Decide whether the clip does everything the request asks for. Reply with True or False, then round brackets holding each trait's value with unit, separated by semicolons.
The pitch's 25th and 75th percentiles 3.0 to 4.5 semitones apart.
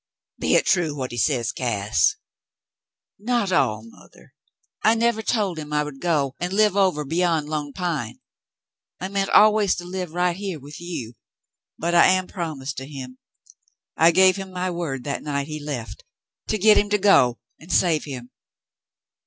False (5.1 semitones)